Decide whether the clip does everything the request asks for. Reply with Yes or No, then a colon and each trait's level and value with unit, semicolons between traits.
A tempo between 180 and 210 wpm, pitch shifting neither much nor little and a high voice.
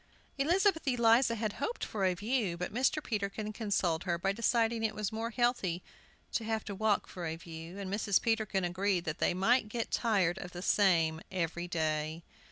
Yes: average, 190 wpm; average, 4.5 semitones; high, 200 Hz